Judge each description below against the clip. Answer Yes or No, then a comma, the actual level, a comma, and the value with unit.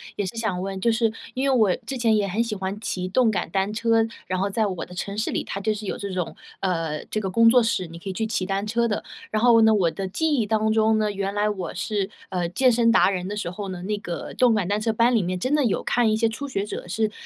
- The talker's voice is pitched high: Yes, high, 210 Hz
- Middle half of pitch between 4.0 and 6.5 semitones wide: No, average, 3.1 semitones